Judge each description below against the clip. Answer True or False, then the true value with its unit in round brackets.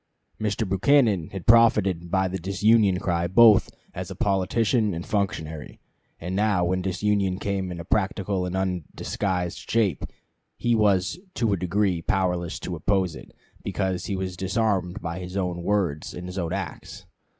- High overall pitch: False (95 Hz)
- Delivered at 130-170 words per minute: True (155 wpm)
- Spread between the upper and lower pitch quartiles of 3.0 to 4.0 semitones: False (2.4 semitones)